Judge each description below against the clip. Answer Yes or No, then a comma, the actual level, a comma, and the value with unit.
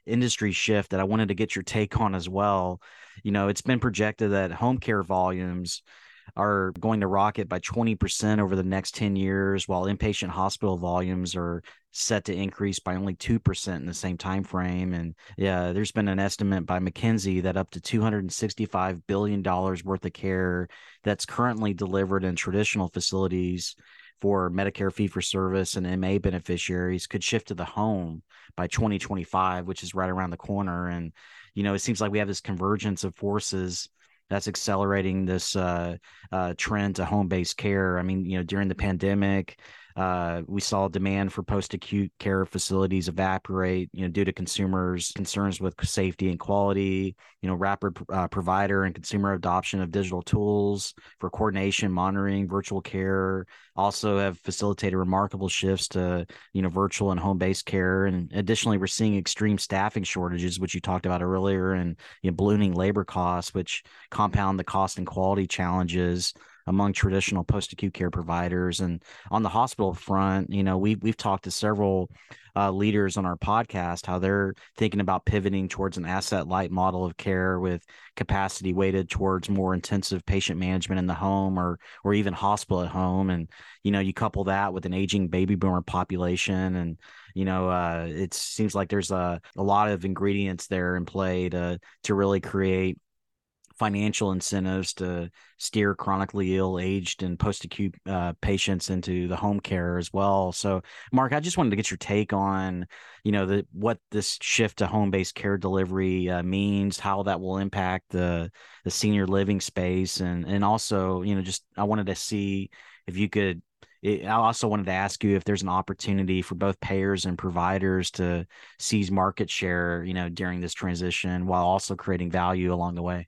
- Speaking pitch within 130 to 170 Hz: No, very low, 95 Hz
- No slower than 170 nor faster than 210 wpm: Yes, average, 180 wpm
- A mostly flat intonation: Yes, narrow, 1.6 semitones